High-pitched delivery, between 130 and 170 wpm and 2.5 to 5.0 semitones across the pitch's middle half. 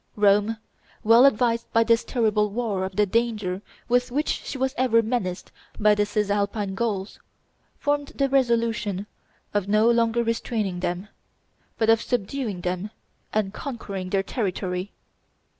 Yes: high, 215 Hz; average, 140 wpm; average, 3.0 semitones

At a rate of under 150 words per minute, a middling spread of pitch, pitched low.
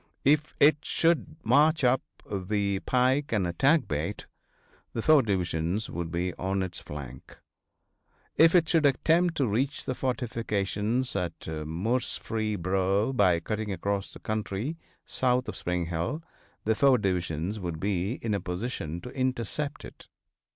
No: average, 140 wpm; wide, 6.3 semitones; low, 105 Hz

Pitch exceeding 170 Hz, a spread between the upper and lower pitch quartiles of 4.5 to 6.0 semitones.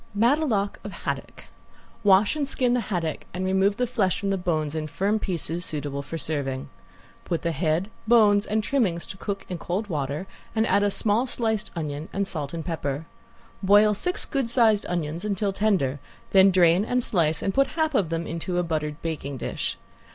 Yes: high, 190 Hz; average, 4.8 semitones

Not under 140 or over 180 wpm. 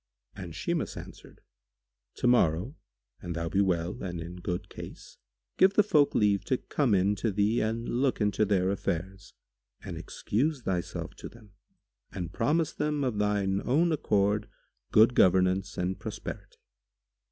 Yes: average, 145 wpm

